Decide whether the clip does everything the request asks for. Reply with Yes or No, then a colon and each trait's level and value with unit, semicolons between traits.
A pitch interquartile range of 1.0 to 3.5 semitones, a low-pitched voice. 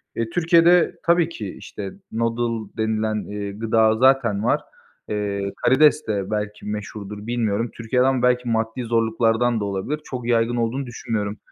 Yes: average, 2.8 semitones; low, 115 Hz